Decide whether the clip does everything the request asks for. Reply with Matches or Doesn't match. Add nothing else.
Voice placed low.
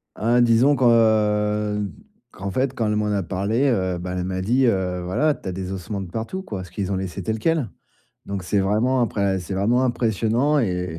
Matches